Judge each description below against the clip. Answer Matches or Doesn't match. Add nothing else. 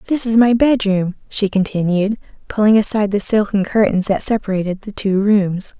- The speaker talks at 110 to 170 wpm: Matches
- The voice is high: Matches